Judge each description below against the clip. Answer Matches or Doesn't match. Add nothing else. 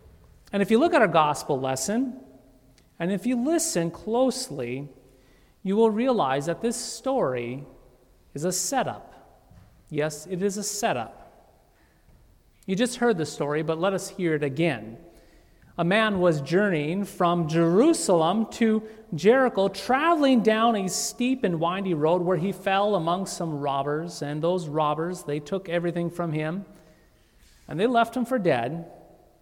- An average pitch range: Doesn't match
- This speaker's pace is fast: Doesn't match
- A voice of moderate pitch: Matches